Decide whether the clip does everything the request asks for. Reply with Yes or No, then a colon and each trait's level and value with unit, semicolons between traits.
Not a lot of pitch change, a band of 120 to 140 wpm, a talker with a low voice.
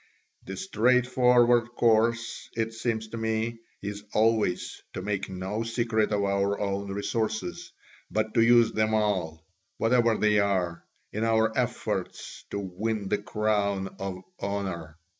Yes: narrow, 2.3 semitones; slow, 135 wpm; low, 110 Hz